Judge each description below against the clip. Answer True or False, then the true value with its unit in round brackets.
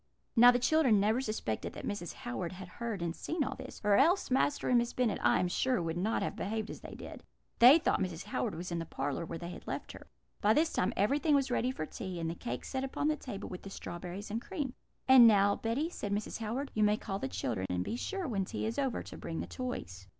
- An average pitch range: False (6.3 semitones)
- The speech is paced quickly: True (255 wpm)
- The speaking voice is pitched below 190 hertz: False (215 Hz)